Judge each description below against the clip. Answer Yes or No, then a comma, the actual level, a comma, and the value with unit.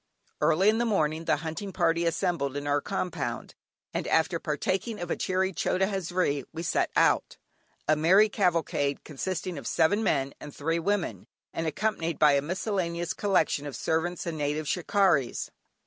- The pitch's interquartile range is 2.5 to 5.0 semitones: Yes, average, 3.9 semitones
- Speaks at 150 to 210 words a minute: Yes, average, 165 wpm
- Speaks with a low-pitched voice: No, medium, 165 Hz